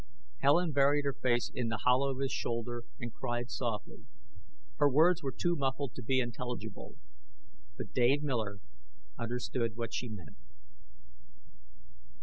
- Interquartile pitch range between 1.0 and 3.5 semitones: Yes, average, 2.8 semitones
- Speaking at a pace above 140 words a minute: No, slow, 135 wpm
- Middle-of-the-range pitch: No, low, 125 Hz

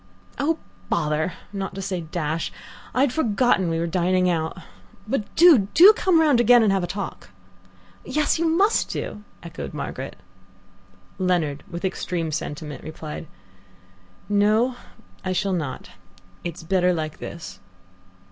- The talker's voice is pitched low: No, medium, 185 Hz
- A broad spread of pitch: Yes, wide, 6.6 semitones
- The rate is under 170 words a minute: Yes, average, 140 wpm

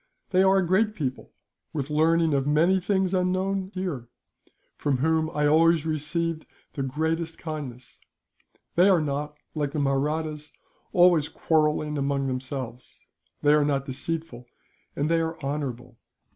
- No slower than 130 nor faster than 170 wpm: Yes, average, 140 wpm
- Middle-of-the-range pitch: Yes, medium, 155 Hz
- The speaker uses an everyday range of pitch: Yes, average, 3.0 semitones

